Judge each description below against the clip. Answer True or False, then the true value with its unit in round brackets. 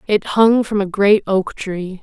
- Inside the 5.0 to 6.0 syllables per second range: False (3.8 syllables/s)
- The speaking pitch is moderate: False (200 Hz)